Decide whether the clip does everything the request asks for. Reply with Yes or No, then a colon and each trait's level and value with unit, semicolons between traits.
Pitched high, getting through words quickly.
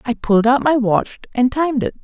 Yes: very high, 250 Hz; fast, 235 wpm